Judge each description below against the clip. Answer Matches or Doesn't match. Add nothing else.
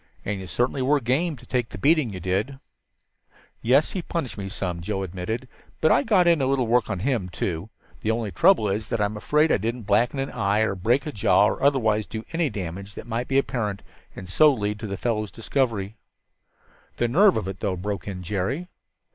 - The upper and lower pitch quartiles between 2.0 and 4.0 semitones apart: Doesn't match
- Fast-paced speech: Matches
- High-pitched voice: Doesn't match